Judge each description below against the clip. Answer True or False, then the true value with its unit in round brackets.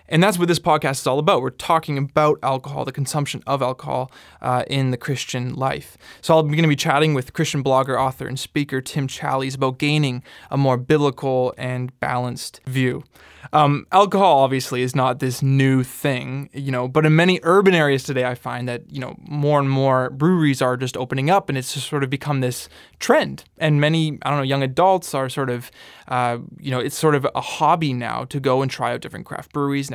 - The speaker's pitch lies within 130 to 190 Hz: True (135 Hz)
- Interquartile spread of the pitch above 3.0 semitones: False (2.7 semitones)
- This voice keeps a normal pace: False (215 wpm)